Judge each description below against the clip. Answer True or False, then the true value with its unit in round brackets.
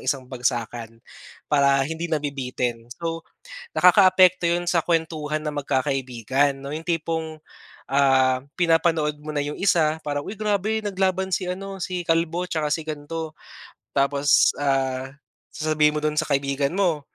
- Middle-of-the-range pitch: True (155 Hz)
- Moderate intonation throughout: True (3.6 semitones)